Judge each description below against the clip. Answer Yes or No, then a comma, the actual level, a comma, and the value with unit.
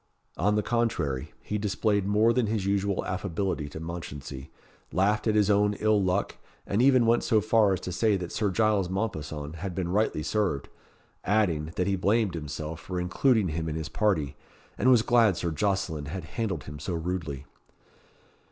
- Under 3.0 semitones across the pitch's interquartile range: No, average, 4.7 semitones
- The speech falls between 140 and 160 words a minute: No, average, 180 wpm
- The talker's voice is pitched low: Yes, very low, 95 Hz